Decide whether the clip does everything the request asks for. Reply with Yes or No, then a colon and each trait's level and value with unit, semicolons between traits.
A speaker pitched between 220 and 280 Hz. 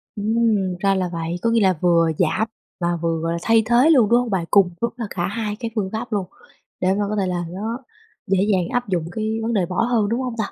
No: high, 205 Hz